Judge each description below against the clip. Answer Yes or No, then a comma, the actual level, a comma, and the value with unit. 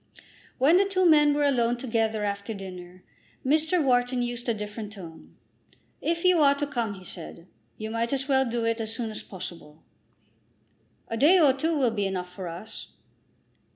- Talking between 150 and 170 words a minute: No, average, 180 wpm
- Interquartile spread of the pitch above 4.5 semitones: Yes, wide, 5.6 semitones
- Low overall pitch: No, high, 235 Hz